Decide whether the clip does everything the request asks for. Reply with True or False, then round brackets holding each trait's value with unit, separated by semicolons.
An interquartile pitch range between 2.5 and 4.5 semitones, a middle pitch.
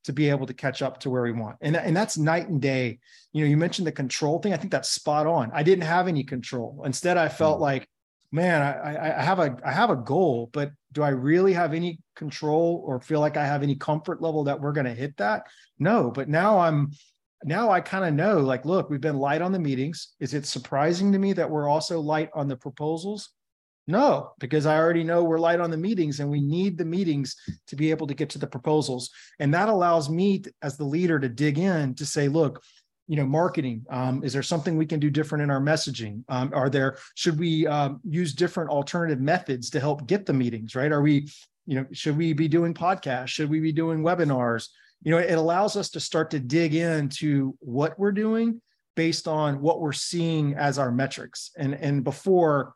True (3.1 semitones; 150 Hz)